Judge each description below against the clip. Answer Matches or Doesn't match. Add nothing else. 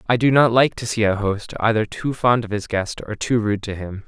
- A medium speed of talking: Doesn't match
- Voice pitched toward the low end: Matches